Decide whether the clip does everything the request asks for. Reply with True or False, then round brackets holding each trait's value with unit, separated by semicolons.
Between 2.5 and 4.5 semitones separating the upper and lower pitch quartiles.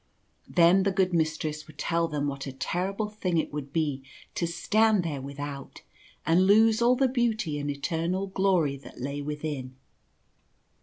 False (5.1 semitones)